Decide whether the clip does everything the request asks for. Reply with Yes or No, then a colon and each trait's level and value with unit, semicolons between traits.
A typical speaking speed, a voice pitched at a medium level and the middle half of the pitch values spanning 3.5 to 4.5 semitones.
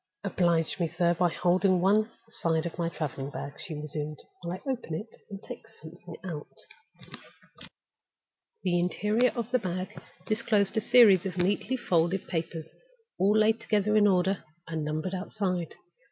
Yes: average, 155 wpm; medium, 180 Hz; average, 3.9 semitones